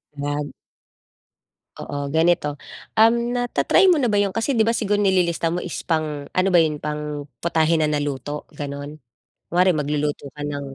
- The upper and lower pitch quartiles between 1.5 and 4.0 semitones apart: No, average, 4.5 semitones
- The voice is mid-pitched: Yes, medium, 160 Hz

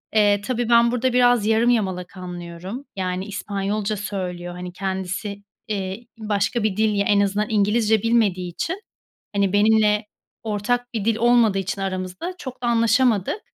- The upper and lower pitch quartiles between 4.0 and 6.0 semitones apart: No, average, 3.2 semitones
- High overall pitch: Yes, high, 210 Hz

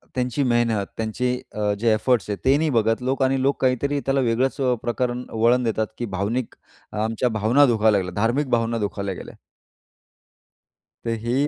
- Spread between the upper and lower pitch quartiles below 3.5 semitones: Yes, average, 2.9 semitones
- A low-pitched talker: Yes, low, 120 Hz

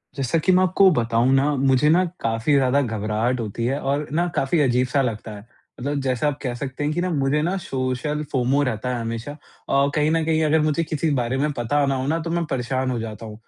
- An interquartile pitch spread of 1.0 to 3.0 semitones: No, average, 3.6 semitones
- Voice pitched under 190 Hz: Yes, low, 135 Hz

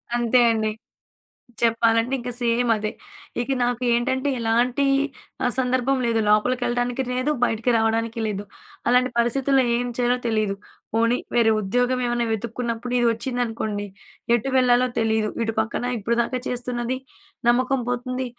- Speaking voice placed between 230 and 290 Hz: Yes, high, 240 Hz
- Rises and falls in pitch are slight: Yes, narrow, 1.7 semitones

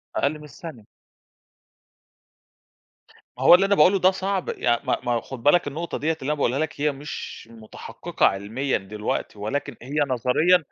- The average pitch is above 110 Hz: Yes, medium, 140 Hz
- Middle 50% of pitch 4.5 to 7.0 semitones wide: Yes, wide, 5.5 semitones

